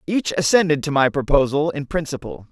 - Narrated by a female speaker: No, male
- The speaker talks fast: No, average, 165 wpm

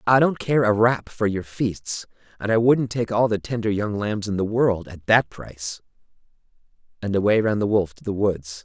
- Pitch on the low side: Yes, low, 105 Hz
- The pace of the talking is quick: Yes, fast, 215 wpm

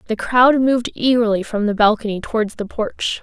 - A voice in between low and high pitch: No, high, 225 Hz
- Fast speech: No, average, 185 wpm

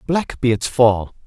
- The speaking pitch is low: Yes, low, 120 Hz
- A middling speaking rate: Yes, average, 190 wpm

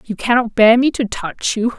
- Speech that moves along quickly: Yes, fast, 235 wpm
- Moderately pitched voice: No, high, 230 Hz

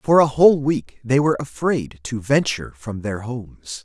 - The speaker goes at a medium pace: Yes, average, 190 wpm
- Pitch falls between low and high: No, low, 125 Hz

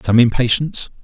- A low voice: Yes, low, 120 Hz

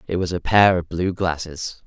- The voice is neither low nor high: No, very low, 90 Hz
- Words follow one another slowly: No, fast, 225 wpm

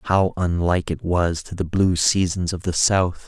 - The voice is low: Yes, very low, 90 Hz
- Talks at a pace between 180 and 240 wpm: Yes, average, 200 wpm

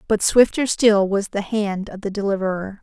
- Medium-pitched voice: No, high, 205 Hz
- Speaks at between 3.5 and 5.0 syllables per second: Yes, 4.9 syllables/s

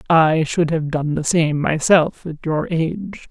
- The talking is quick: No, average, 180 wpm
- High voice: No, medium, 160 Hz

